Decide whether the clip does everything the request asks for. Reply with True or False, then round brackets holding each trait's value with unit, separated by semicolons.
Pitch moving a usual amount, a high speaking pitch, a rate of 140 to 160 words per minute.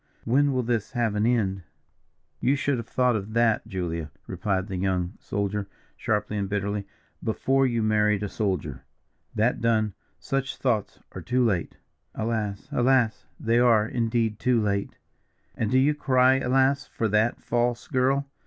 False (3.6 semitones; 110 Hz; 155 wpm)